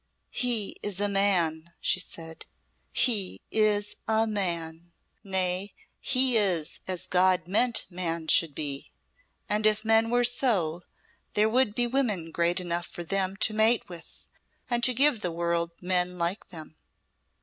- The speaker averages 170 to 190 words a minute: No, average, 150 wpm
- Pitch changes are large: No, average, 4.3 semitones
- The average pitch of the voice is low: No, high, 190 Hz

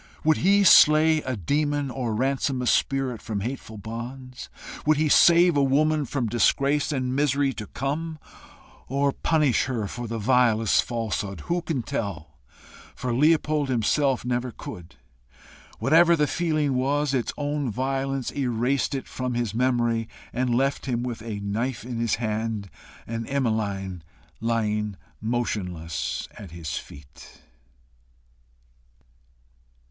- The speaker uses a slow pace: Yes, slow, 130 wpm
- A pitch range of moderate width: Yes, average, 4.1 semitones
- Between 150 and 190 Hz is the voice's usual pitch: No, low, 125 Hz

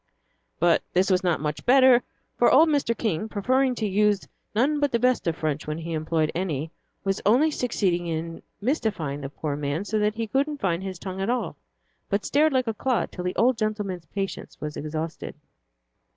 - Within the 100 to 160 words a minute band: No, average, 195 wpm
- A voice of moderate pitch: No, high, 200 Hz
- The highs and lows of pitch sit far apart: Yes, wide, 6.7 semitones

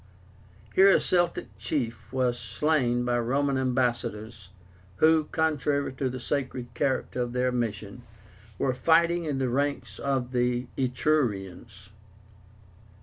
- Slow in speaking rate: Yes, slow, 120 wpm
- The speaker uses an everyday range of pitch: Yes, average, 3.0 semitones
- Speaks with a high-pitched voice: No, low, 130 Hz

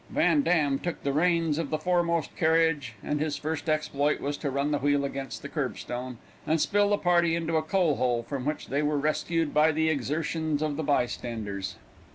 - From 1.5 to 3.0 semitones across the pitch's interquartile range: Yes, average, 2.7 semitones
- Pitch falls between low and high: Yes, medium, 150 Hz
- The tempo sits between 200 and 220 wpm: Yes, fast, 205 wpm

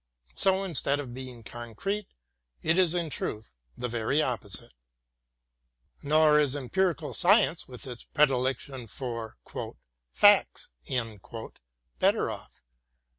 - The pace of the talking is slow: Yes, slow, 105 wpm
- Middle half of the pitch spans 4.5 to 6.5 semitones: Yes, average, 5.0 semitones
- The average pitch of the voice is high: No, low, 135 Hz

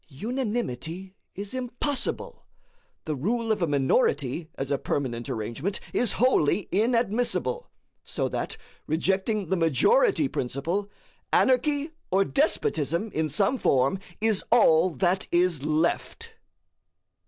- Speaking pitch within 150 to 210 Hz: Yes, high, 190 Hz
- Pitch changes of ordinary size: No, wide, 7.7 semitones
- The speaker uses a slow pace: Yes, slow, 110 wpm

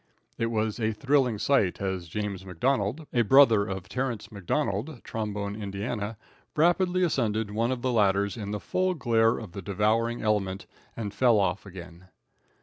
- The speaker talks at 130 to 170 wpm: Yes, average, 155 wpm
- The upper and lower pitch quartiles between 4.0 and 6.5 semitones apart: No, average, 3.5 semitones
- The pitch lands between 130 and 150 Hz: No, low, 110 Hz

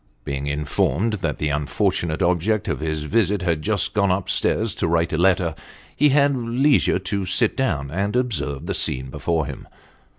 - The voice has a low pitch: Yes, very low, 90 Hz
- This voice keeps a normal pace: Yes, average, 175 wpm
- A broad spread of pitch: Yes, wide, 5.8 semitones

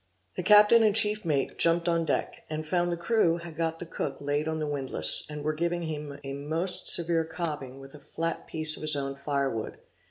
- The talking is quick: Yes, fast, 220 wpm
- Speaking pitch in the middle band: Yes, medium, 160 Hz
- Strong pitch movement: No, average, 2.8 semitones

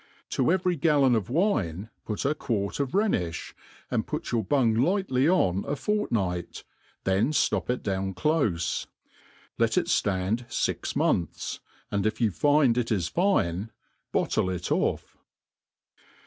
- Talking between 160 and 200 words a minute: No, slow, 135 wpm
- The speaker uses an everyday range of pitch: No, wide, 7.5 semitones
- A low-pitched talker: Yes, low, 115 Hz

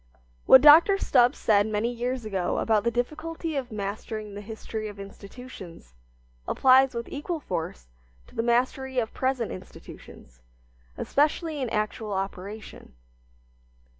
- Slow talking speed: Yes, slow, 130 wpm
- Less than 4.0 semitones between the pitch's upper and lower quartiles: No, average, 4.3 semitones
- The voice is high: Yes, high, 230 Hz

